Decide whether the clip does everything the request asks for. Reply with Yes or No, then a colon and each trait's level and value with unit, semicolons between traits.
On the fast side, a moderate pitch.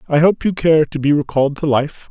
Yes: fast, 255 wpm; medium, 150 Hz